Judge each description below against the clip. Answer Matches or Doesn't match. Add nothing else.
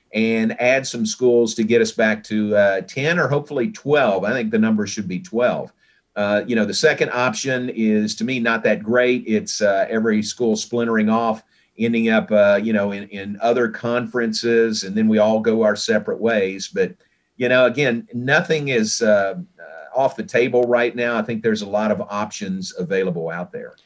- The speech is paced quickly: Doesn't match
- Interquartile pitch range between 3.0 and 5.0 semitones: Doesn't match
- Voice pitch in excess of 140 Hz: Doesn't match